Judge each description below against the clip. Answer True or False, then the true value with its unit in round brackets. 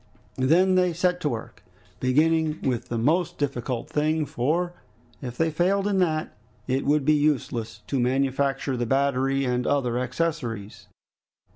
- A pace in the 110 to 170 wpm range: True (145 wpm)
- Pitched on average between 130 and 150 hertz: True (140 Hz)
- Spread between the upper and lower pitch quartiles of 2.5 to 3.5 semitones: False (4.3 semitones)